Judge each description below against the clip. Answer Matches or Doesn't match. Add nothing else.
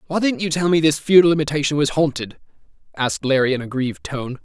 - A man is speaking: Matches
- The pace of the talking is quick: Matches